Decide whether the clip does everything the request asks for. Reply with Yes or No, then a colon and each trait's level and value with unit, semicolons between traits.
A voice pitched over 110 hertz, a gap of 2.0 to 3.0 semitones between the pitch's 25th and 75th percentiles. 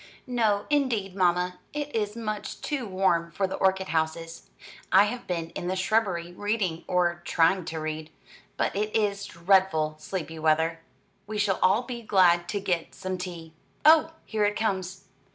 No: high, 190 Hz; average, 3.7 semitones